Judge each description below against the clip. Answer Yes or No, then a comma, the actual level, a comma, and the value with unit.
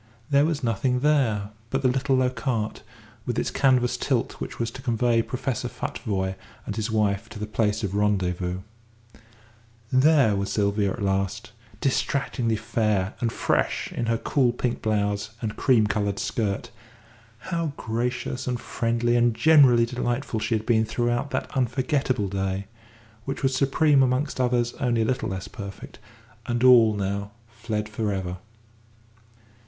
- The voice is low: Yes, low, 115 Hz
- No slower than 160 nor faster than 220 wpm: No, average, 150 wpm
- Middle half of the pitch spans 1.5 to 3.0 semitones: No, average, 3.5 semitones